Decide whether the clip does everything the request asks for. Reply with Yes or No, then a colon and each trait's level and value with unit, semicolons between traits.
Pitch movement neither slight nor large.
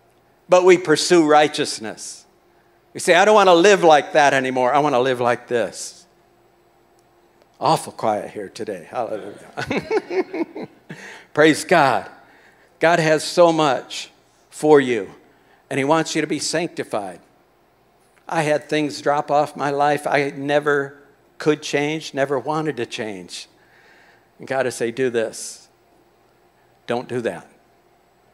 Yes: average, 3.1 semitones